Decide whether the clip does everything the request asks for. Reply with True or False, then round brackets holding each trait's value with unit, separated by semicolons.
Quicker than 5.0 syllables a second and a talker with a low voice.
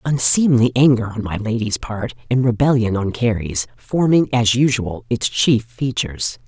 False (4.5 syllables/s; 120 Hz)